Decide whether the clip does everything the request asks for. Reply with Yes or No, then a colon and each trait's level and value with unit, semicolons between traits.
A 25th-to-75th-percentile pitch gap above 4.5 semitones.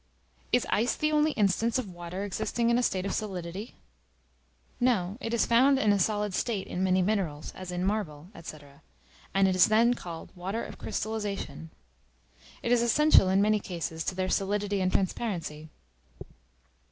No: average, 3.7 semitones